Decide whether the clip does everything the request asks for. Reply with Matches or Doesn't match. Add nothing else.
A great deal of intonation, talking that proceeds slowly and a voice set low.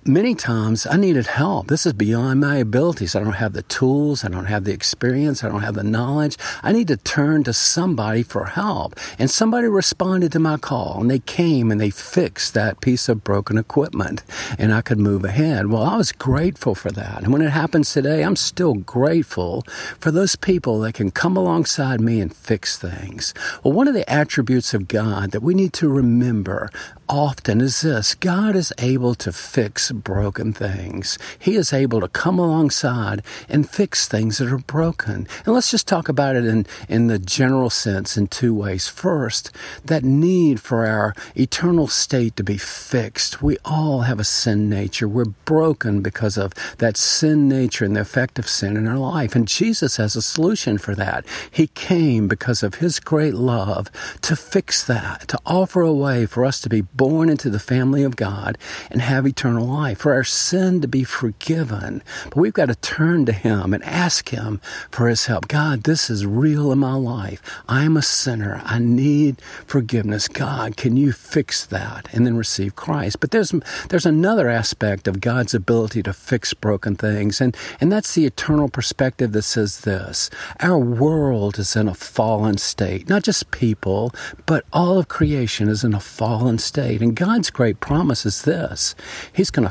Doesn't match